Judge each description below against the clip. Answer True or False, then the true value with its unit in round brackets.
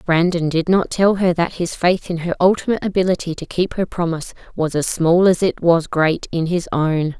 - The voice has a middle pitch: True (170 Hz)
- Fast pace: True (215 wpm)